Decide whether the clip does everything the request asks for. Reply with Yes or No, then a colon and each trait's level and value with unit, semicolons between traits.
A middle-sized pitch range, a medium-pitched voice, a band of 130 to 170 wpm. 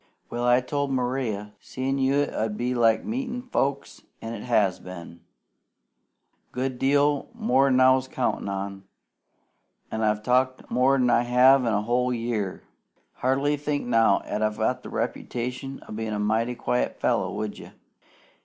No: average, 3.6 semitones; low, 125 Hz; average, 150 wpm